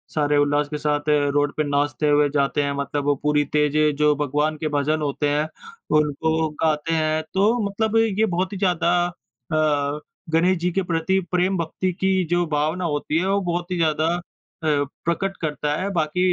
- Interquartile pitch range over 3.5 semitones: No, average, 3.2 semitones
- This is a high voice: No, medium, 155 Hz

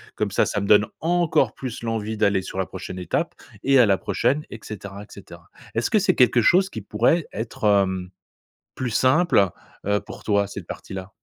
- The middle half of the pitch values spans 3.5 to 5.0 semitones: Yes, average, 4.4 semitones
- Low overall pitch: Yes, low, 105 Hz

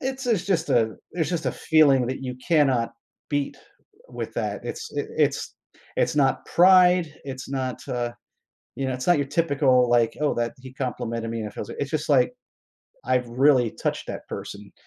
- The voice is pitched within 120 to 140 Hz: Yes, low, 135 Hz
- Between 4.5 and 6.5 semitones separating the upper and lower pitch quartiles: Yes, average, 5.1 semitones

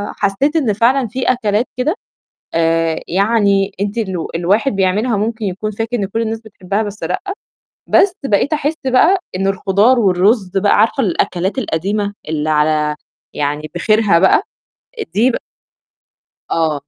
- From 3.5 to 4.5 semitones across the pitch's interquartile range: Yes, average, 4.0 semitones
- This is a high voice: Yes, high, 205 Hz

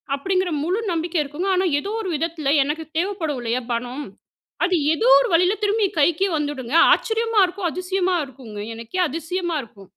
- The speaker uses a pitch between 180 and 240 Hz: No, very high, 330 Hz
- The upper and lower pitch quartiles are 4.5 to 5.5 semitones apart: Yes, average, 5.0 semitones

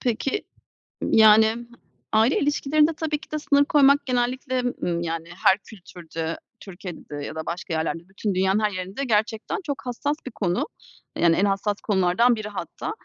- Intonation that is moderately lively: No, wide, 6.6 semitones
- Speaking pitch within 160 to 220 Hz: Yes, high, 215 Hz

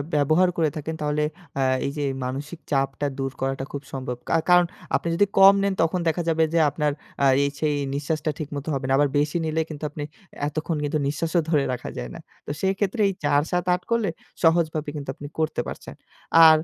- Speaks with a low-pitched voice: No, medium, 155 Hz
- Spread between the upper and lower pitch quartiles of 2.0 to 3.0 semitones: Yes, average, 2.7 semitones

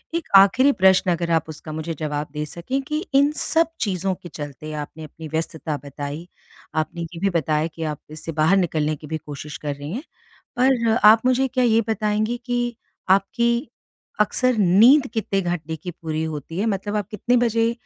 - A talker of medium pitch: Yes, medium, 180 Hz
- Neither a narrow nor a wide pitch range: No, wide, 6.8 semitones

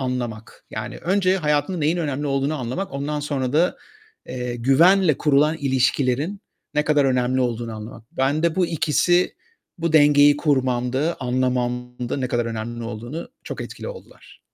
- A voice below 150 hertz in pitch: Yes, low, 135 Hz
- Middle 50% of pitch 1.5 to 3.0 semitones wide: No, average, 3.9 semitones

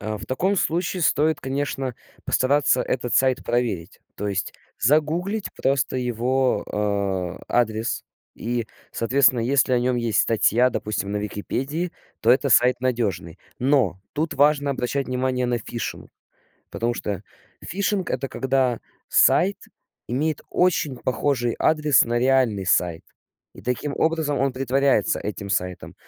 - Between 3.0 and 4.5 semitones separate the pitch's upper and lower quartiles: Yes, average, 3.6 semitones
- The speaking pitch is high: No, low, 130 Hz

